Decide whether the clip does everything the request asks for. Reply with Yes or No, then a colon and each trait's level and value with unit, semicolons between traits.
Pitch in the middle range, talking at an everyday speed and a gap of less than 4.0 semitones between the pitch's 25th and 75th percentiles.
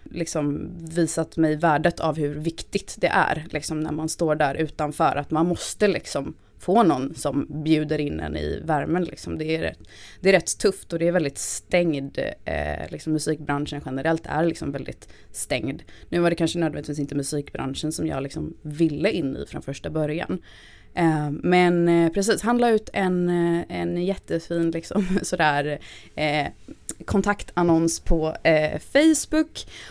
Yes: medium, 160 Hz; average, 160 wpm; average, 2.7 semitones